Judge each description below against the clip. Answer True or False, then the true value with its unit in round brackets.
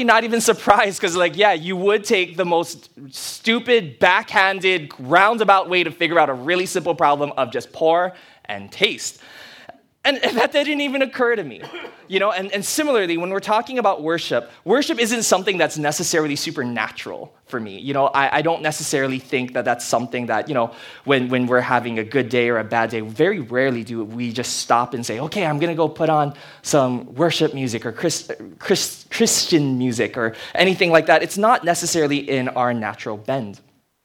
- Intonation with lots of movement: True (6.8 semitones)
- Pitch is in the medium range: True (155 Hz)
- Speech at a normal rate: True (190 wpm)